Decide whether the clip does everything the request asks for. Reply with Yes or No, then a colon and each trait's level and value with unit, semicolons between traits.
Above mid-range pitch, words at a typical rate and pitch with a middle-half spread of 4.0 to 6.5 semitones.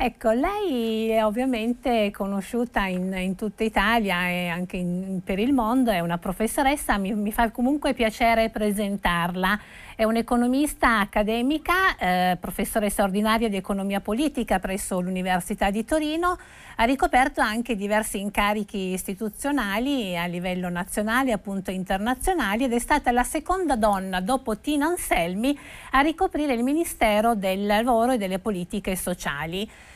Yes: high, 220 Hz; average, 135 wpm; average, 4.6 semitones